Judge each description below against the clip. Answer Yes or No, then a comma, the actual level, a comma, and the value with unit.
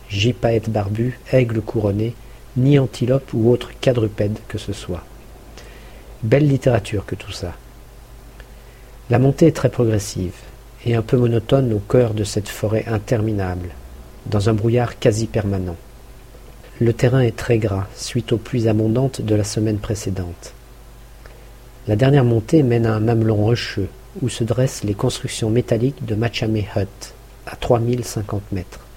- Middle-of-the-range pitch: No, low, 115 Hz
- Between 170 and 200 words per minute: No, slow, 145 wpm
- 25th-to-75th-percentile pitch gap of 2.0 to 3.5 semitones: Yes, average, 2.9 semitones